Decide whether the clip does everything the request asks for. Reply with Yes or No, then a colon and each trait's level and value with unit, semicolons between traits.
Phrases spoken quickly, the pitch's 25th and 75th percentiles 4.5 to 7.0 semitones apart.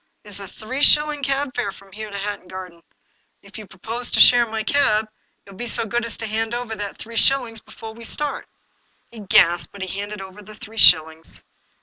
No: fast, 220 wpm; average, 3.3 semitones